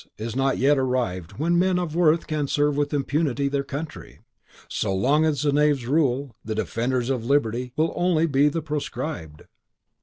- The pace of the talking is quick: No, average, 175 wpm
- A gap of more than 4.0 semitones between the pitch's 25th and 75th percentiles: No, average, 3.5 semitones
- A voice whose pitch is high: No, medium, 140 Hz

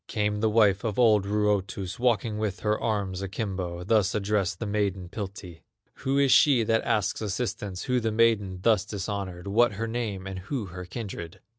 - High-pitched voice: No, low, 105 Hz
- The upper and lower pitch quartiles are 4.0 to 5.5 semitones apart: No, average, 2.7 semitones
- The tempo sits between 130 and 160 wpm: No, average, 175 wpm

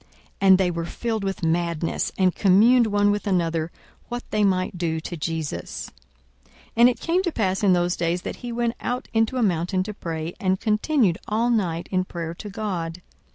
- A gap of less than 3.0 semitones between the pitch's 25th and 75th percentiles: No, average, 4.3 semitones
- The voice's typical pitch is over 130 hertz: Yes, high, 190 Hz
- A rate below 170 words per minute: No, average, 200 wpm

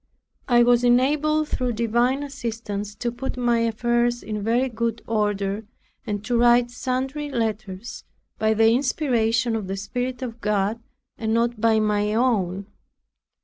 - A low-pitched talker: No, high, 235 Hz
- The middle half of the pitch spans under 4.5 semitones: Yes, narrow, 2.5 semitones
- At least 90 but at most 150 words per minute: Yes, average, 145 wpm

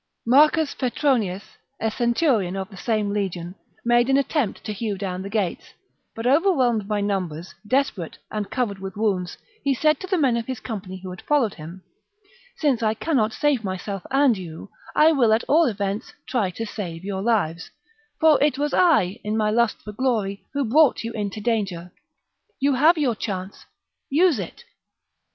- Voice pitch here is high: Yes, high, 220 Hz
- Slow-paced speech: No, average, 180 wpm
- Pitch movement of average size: No, wide, 5.8 semitones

